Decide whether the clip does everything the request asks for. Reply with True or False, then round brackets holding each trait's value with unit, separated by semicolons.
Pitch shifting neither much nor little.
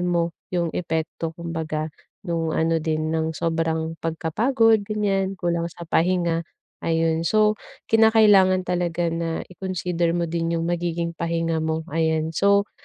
False (2.0 semitones)